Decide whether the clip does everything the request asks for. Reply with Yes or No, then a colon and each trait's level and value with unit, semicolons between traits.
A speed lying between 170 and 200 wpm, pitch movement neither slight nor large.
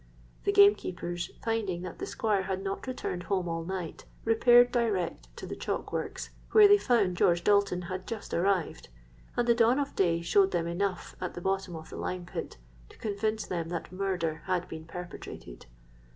Yes: average, 180 wpm; average, 3.5 semitones